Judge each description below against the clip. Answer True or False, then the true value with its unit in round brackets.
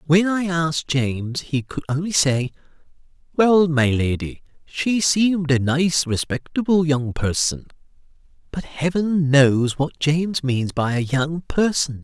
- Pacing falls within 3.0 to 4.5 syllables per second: True (4.0 syllables/s)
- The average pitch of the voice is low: False (150 Hz)